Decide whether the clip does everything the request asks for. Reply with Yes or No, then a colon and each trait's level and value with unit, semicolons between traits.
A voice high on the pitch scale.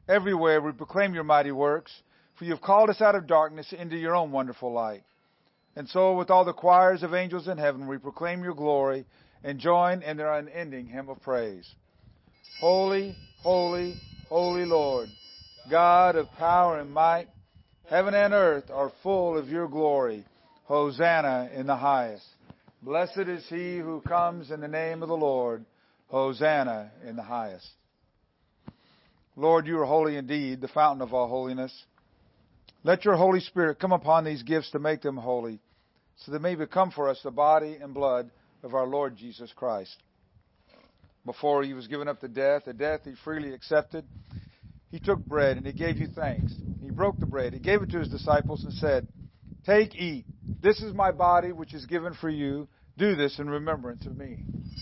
No: medium, 150 Hz